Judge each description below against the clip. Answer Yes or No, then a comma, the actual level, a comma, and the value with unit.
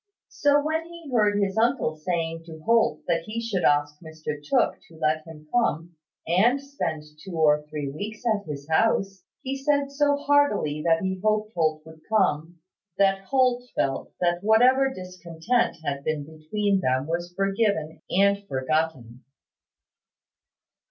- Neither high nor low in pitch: Yes, medium, 180 Hz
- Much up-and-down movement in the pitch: Yes, wide, 6.4 semitones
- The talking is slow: No, average, 150 wpm